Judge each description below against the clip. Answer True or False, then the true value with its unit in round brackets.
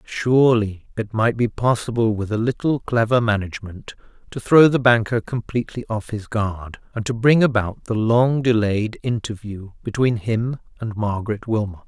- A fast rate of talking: False (155 wpm)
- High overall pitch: False (115 Hz)